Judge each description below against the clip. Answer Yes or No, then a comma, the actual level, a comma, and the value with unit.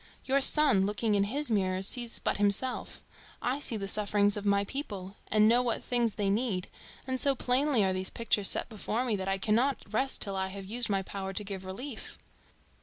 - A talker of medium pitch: No, high, 210 Hz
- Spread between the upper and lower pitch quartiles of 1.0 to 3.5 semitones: No, average, 4.0 semitones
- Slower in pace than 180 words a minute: No, fast, 205 wpm